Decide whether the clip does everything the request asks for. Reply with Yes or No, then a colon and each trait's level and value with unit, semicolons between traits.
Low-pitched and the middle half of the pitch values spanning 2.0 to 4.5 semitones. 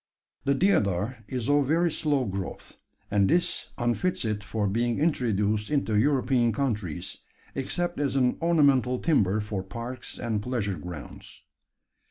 No: low, 120 Hz; average, 5.2 semitones